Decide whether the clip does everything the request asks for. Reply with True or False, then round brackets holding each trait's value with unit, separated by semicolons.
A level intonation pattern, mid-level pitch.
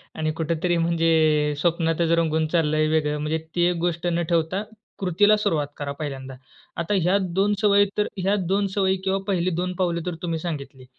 False (3.0 semitones; 170 Hz)